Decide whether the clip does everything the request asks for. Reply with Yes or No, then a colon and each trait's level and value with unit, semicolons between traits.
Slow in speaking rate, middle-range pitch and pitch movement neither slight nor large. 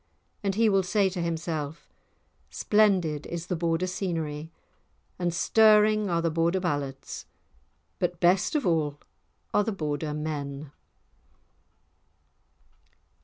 Yes: slow, 115 wpm; medium, 170 Hz; average, 3.9 semitones